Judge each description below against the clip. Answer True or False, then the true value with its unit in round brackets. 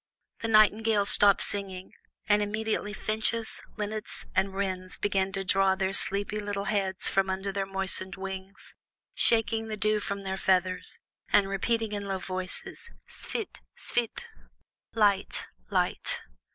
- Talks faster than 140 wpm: False (135 wpm)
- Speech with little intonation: True (1.8 semitones)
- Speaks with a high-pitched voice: True (200 Hz)